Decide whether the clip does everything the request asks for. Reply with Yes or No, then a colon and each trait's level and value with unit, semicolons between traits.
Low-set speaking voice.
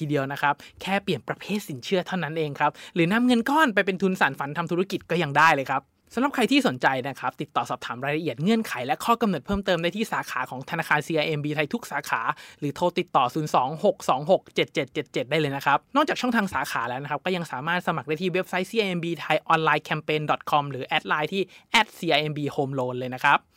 No: medium, 165 Hz